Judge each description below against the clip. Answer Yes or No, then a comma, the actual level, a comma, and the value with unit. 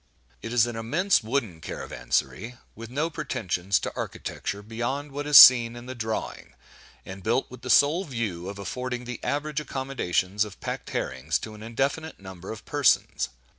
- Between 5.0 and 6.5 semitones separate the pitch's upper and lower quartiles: Yes, average, 5.3 semitones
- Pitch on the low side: Yes, low, 115 Hz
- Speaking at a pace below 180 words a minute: Yes, average, 170 wpm